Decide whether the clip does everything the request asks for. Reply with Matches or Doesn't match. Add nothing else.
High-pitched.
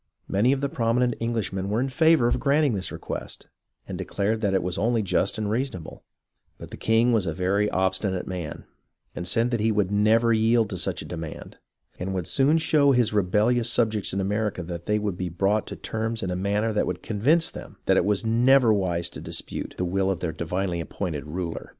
Doesn't match